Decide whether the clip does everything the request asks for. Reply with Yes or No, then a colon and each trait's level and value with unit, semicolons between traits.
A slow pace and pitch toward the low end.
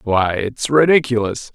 Yes: slow, 115 wpm; low, 120 Hz